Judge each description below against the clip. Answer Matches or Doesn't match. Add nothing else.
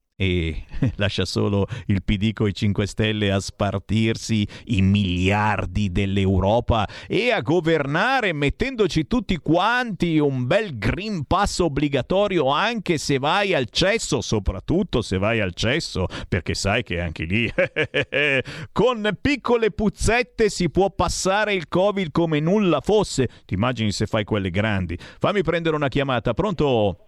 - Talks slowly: Doesn't match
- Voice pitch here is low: Matches